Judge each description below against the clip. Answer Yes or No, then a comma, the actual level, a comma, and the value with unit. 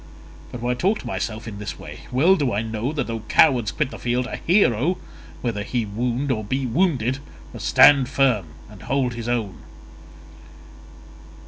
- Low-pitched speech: Yes, low, 120 Hz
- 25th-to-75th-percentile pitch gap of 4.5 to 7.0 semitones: No, average, 3.7 semitones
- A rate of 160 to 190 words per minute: Yes, average, 175 wpm